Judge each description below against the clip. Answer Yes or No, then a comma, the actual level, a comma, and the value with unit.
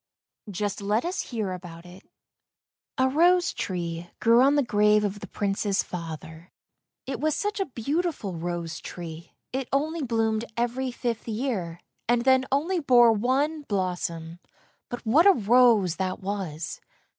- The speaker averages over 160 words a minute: No, average, 145 wpm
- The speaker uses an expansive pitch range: Yes, wide, 6.4 semitones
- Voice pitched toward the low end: No, high, 220 Hz